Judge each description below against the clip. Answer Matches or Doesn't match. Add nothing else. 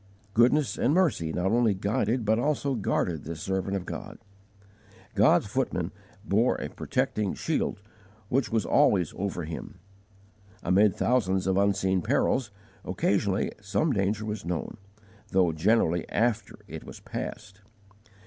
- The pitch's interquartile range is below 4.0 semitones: Matches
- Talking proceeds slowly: Matches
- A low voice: Matches